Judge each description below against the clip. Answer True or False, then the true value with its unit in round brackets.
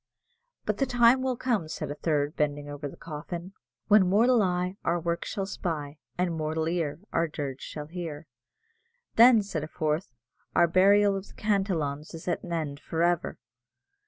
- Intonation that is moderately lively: True (4.3 semitones)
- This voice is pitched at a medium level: True (170 Hz)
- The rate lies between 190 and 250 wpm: False (175 wpm)